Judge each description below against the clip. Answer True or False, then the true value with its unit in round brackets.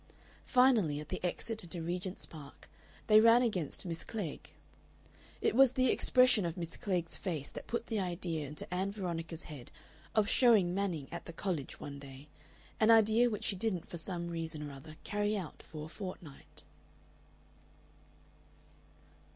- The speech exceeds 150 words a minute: True (160 wpm)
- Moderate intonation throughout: True (5.0 semitones)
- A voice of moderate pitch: True (180 Hz)